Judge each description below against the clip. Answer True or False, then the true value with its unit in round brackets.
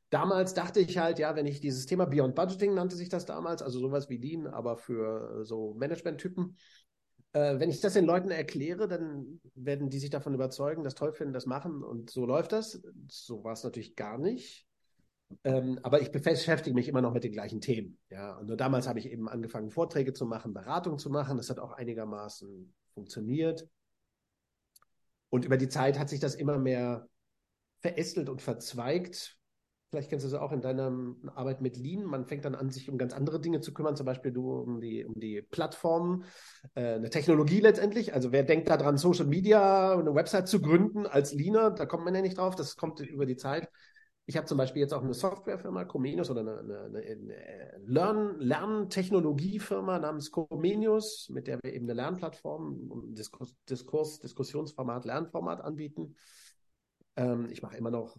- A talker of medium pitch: True (145 Hz)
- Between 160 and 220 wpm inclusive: True (190 wpm)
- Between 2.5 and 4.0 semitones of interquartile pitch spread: False (5.2 semitones)